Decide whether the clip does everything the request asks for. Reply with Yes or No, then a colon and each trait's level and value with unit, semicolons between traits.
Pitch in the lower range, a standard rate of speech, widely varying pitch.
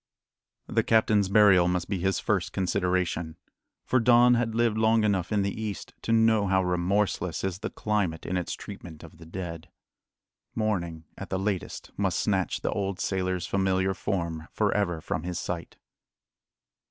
No: very low, 95 Hz; average, 165 wpm; average, 3.1 semitones